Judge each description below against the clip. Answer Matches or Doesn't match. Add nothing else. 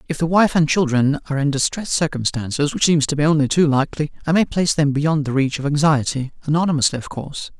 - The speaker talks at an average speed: Doesn't match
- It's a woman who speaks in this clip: Doesn't match